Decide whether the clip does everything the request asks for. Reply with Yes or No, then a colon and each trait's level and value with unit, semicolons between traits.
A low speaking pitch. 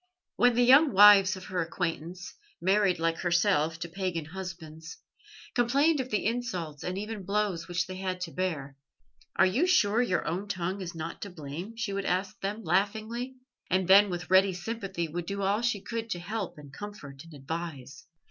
No: medium, 185 Hz